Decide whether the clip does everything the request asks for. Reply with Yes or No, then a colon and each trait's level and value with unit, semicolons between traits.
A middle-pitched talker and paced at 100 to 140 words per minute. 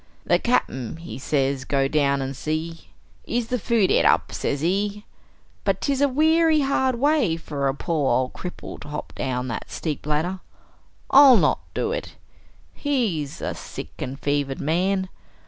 No: medium, 165 Hz; average, 165 wpm